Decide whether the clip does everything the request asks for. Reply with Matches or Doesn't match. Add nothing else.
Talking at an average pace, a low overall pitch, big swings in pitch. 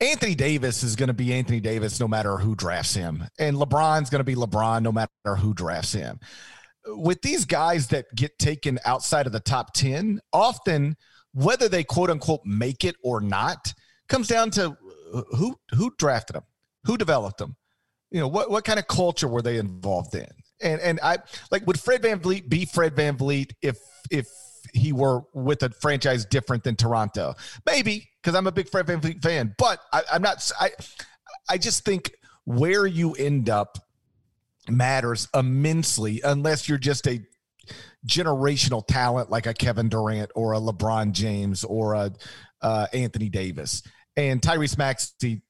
Matches